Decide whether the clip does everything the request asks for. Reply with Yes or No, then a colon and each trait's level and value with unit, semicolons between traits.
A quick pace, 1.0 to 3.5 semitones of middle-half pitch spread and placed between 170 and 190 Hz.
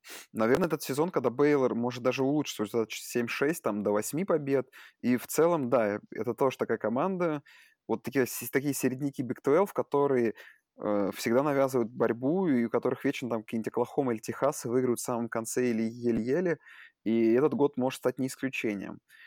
No: fast, 170 wpm; average, 3.1 semitones; low, 125 Hz